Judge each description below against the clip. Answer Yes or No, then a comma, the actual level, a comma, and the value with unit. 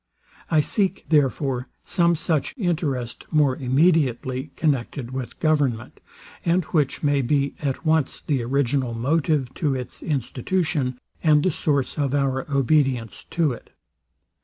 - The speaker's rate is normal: No, slow, 130 wpm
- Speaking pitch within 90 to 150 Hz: Yes, medium, 140 Hz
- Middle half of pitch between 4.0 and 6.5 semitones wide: No, average, 3.3 semitones